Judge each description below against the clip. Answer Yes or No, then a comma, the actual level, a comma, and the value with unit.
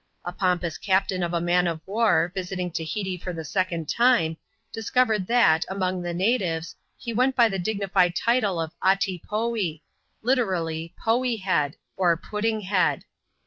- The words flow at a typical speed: Yes, average, 160 wpm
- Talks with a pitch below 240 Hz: Yes, medium, 185 Hz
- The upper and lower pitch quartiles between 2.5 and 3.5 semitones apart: No, average, 4.2 semitones